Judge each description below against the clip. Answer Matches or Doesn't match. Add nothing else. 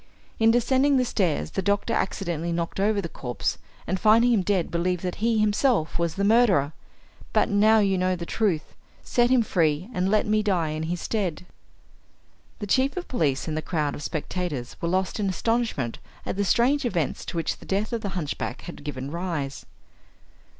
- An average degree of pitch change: Matches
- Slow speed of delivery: Doesn't match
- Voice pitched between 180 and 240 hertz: Matches